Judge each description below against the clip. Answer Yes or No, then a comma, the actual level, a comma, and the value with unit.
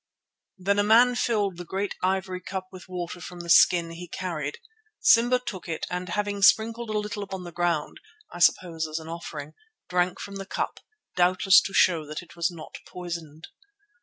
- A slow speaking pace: No, average, 185 wpm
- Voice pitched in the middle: Yes, medium, 180 Hz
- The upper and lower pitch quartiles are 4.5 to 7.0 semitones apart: No, average, 2.7 semitones